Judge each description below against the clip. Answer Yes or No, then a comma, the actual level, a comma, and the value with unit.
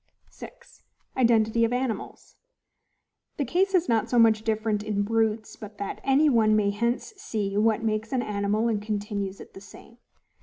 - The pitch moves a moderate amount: No, narrow, 2.1 semitones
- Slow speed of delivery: No, average, 165 wpm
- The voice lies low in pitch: No, high, 220 Hz